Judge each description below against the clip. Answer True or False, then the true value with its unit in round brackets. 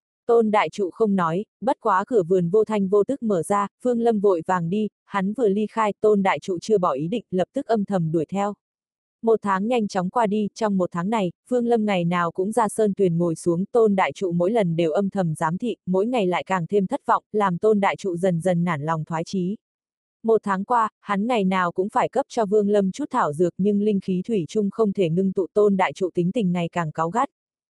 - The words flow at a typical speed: False (255 wpm)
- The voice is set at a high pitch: True (200 Hz)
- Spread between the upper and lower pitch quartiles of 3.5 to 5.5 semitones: False (3.0 semitones)